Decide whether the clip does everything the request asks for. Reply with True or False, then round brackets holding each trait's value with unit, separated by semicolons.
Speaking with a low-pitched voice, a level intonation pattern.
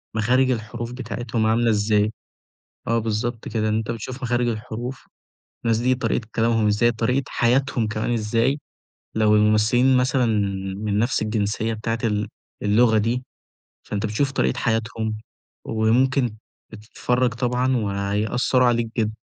True (115 Hz; 2.3 semitones)